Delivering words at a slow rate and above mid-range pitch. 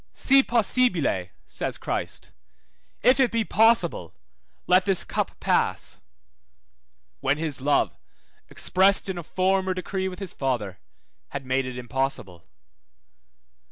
No: slow, 120 wpm; medium, 180 Hz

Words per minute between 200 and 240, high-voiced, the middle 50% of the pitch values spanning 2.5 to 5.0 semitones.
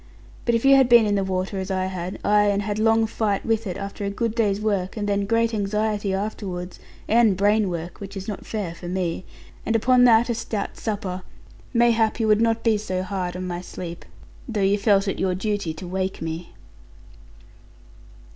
Yes: fast, 205 wpm; high, 205 Hz; average, 2.9 semitones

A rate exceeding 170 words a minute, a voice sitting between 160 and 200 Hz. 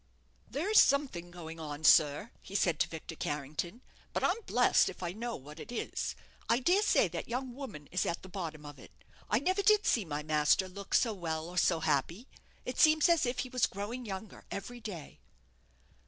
Yes: average, 200 wpm; high, 190 Hz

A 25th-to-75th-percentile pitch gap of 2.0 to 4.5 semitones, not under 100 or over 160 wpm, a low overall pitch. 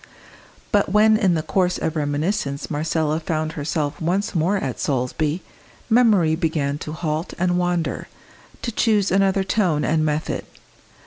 No: average, 4.0 semitones; average, 140 wpm; medium, 165 Hz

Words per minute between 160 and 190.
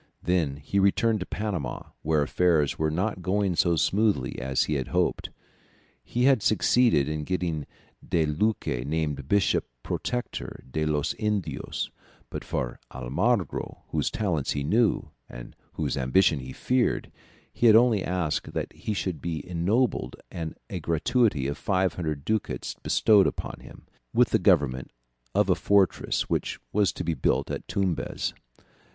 No: average, 150 wpm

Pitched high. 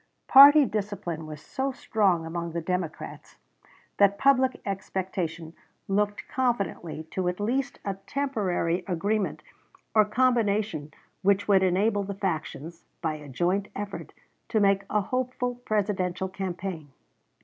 Yes: high, 195 Hz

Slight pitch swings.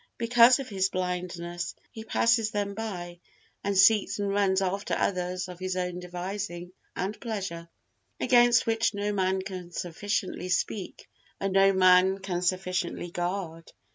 Yes: narrow, 2.3 semitones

